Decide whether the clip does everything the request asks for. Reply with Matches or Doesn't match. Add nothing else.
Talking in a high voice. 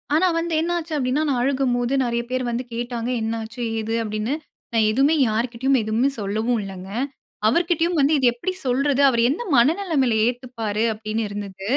Matches